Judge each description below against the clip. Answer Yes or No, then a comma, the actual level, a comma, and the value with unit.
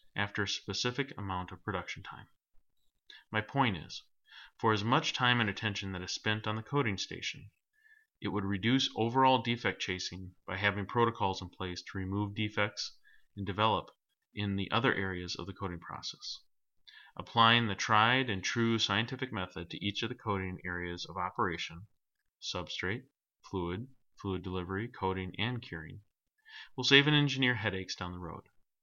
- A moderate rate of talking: Yes, average, 160 wpm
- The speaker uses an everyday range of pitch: Yes, average, 3.9 semitones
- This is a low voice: Yes, low, 105 Hz